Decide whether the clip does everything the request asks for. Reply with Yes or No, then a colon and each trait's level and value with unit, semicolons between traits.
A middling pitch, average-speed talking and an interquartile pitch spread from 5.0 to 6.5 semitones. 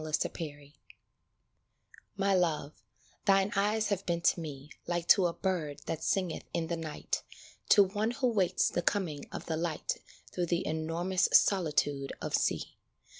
No: medium, 170 Hz; average, 155 wpm; average, 3.7 semitones